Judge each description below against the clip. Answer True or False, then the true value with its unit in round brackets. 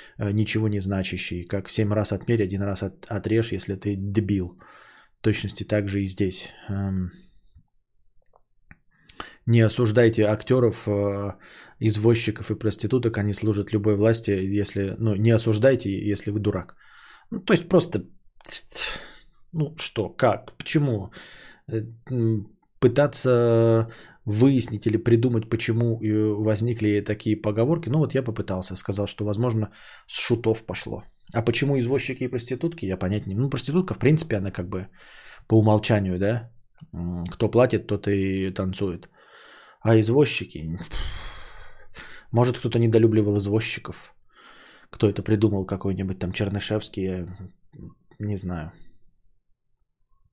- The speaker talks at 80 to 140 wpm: True (120 wpm)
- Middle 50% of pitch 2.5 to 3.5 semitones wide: True (2.8 semitones)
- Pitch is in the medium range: False (110 Hz)